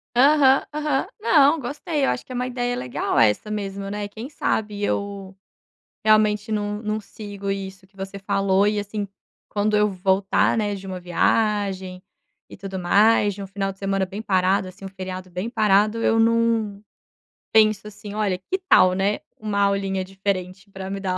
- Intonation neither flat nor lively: No, narrow, 1.9 semitones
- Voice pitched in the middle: No, high, 200 Hz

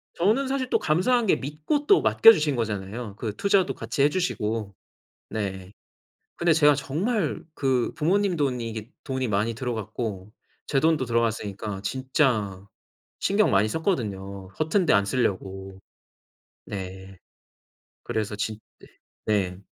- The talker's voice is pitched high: No, low, 120 Hz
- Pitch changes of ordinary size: No, wide, 7.7 semitones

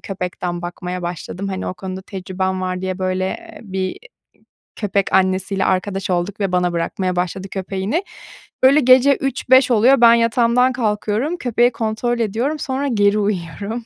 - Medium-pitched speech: No, high, 200 Hz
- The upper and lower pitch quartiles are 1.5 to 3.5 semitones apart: No, average, 4.4 semitones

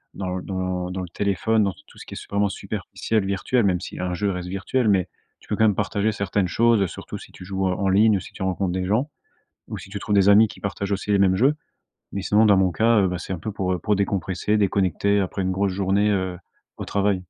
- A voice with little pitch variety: Yes, narrow, 1.8 semitones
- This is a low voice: Yes, low, 100 Hz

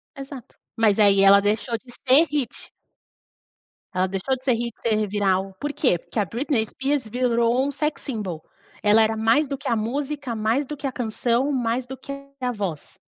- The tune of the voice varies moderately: Yes, average, 4.0 semitones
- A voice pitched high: Yes, high, 235 Hz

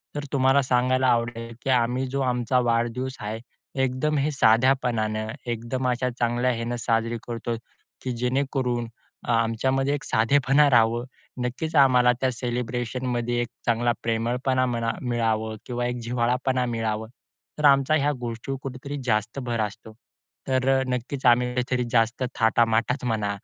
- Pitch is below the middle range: Yes, low, 125 Hz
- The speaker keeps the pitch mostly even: Yes, narrow, 2.0 semitones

